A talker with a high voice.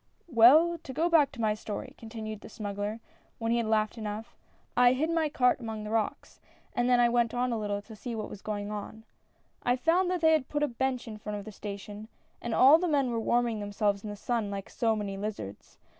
Yes: high, 225 Hz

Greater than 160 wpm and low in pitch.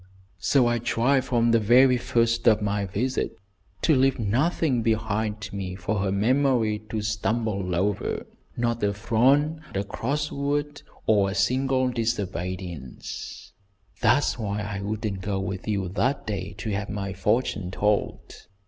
No: average, 145 wpm; low, 110 Hz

